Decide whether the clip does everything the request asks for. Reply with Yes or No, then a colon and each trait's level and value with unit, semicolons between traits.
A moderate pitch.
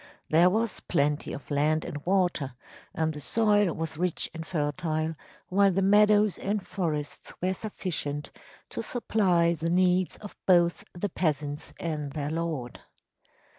Yes: medium, 170 Hz